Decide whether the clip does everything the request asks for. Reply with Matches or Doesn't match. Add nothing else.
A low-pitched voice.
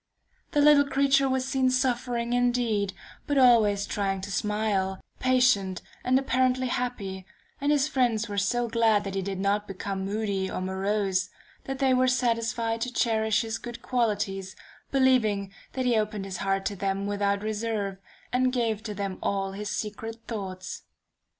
Doesn't match